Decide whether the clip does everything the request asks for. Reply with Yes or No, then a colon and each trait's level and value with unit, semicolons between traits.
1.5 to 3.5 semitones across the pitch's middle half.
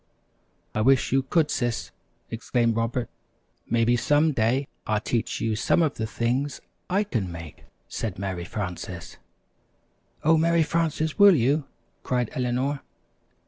No: average, 4.8 semitones